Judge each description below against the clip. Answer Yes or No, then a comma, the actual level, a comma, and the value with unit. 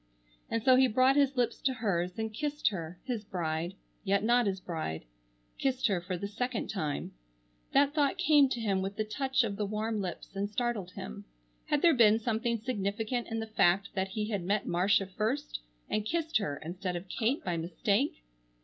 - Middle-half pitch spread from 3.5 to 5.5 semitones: Yes, average, 4.6 semitones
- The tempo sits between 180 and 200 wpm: Yes, average, 195 wpm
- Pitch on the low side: No, high, 215 Hz